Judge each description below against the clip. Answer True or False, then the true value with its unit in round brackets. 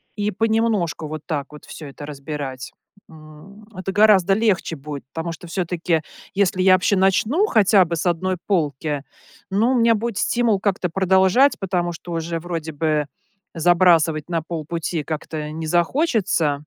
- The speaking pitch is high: False (175 Hz)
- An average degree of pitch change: True (4.1 semitones)